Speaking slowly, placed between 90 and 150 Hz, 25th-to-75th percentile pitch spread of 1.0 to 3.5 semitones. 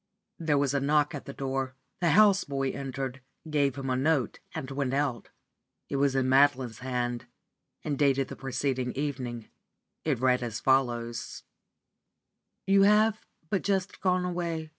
No: average, 155 wpm; low, 135 Hz; average, 3.1 semitones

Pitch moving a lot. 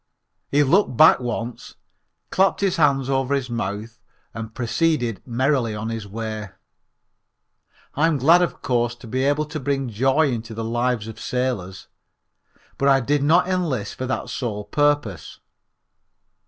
No: average, 4.3 semitones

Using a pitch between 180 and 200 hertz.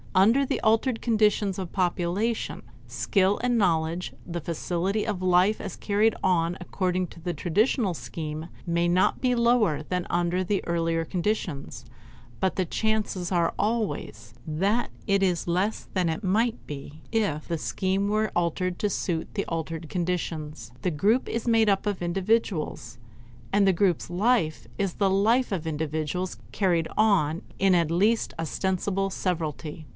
Yes: medium, 185 Hz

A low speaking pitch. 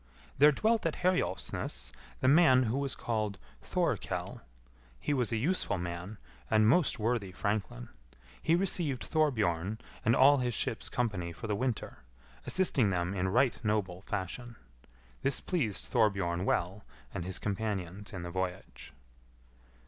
Yes: low, 110 Hz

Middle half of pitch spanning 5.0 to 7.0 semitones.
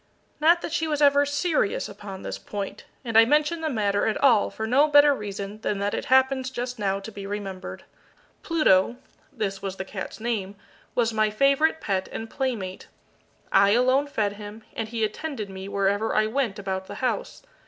Yes: wide, 5.4 semitones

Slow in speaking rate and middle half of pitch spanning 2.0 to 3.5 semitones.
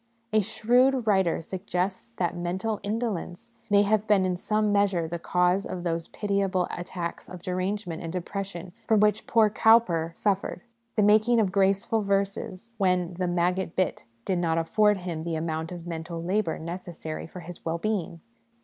No: average, 165 wpm; average, 3.2 semitones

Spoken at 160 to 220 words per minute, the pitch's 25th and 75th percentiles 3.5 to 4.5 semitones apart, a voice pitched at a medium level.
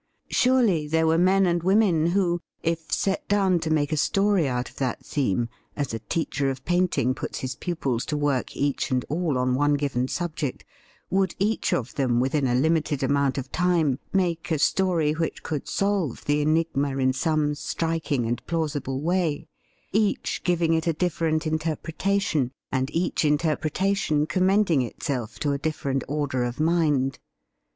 Yes: average, 165 wpm; average, 4.2 semitones; medium, 155 Hz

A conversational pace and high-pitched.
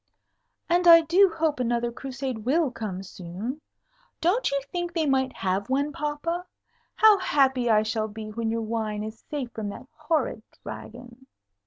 Yes: average, 160 wpm; very high, 260 Hz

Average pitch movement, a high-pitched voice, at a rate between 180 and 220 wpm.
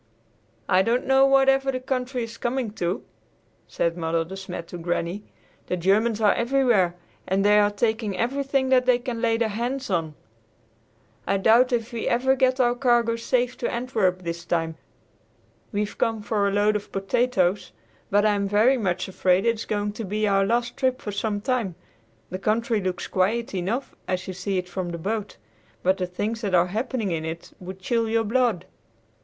Yes: average, 4.4 semitones; high, 210 Hz; average, 190 wpm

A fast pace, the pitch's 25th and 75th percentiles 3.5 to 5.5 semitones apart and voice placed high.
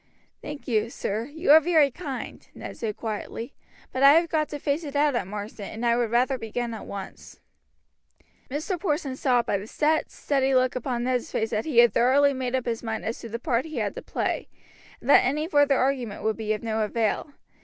Yes: fast, 220 wpm; average, 4.2 semitones; very high, 255 Hz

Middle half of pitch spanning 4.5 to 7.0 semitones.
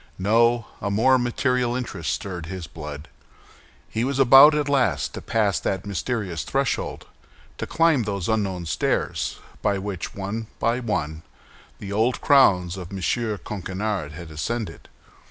Yes: average, 5.0 semitones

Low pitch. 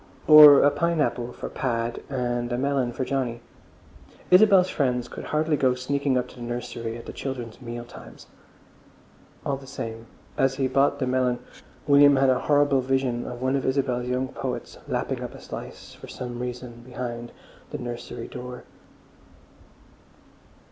Yes: low, 125 Hz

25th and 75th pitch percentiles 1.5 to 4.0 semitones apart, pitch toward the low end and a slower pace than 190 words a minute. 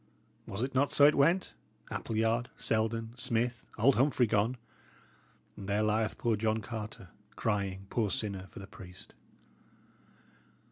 Yes: average, 2.7 semitones; low, 110 Hz; slow, 135 wpm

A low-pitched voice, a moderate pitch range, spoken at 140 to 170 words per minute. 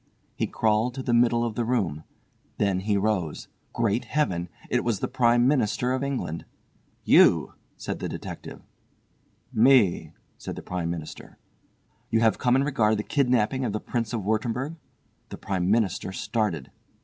Yes: low, 115 Hz; average, 3.8 semitones; average, 160 wpm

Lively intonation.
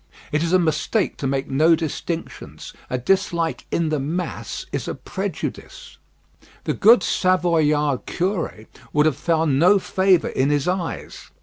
No: average, 3.6 semitones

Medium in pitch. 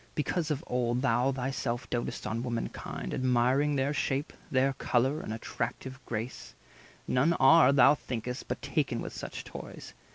No: low, 130 Hz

